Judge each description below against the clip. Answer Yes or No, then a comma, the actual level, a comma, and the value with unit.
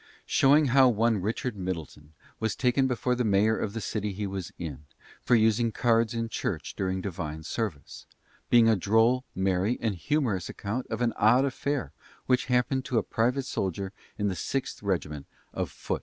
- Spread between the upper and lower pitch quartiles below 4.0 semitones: No, average, 4.3 semitones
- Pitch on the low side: Yes, low, 110 Hz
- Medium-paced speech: Yes, average, 175 wpm